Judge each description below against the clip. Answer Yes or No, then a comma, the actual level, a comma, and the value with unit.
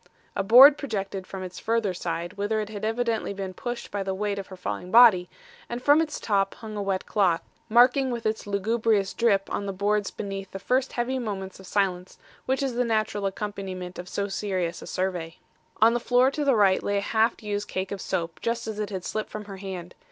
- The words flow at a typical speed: No, fast, 220 wpm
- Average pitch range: Yes, average, 3.2 semitones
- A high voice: Yes, high, 205 Hz